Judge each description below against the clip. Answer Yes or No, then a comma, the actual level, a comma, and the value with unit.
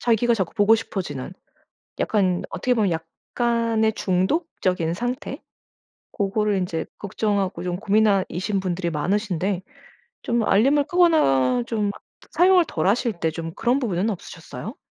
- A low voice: No, high, 200 Hz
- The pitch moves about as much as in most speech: Yes, average, 4.5 semitones